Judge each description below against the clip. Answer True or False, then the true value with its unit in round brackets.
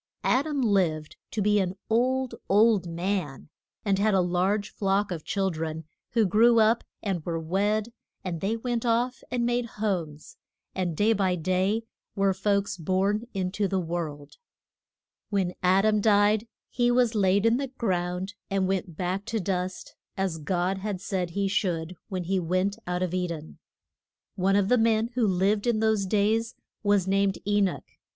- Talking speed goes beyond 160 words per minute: True (175 wpm)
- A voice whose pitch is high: True (195 Hz)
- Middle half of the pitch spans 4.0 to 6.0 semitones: False (3.1 semitones)